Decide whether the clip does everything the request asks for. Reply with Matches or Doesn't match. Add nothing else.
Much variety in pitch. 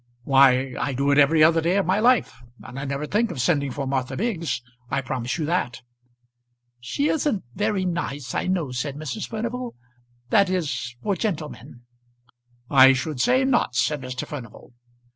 Matches